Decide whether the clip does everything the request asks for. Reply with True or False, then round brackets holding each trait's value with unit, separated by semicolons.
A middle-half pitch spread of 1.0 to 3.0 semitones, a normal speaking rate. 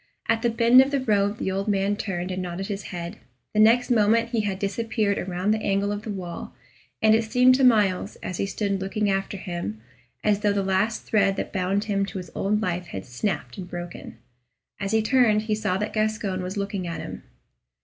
False (2.4 semitones; 215 wpm)